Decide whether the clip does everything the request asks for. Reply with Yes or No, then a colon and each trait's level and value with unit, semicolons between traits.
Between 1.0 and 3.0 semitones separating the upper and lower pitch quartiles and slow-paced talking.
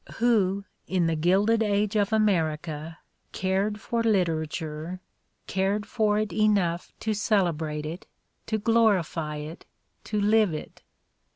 No: average, 4.5 semitones; slow, 120 wpm